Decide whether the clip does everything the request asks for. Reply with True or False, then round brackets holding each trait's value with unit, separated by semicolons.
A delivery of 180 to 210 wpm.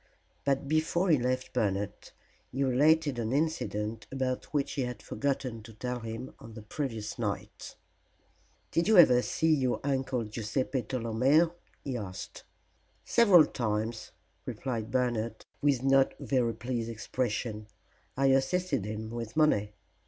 False (135 wpm)